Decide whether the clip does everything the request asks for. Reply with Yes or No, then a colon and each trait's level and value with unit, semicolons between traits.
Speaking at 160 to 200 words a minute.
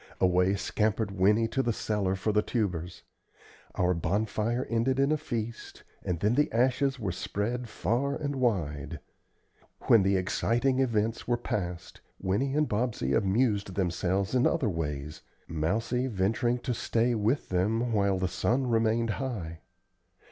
No: average, 145 wpm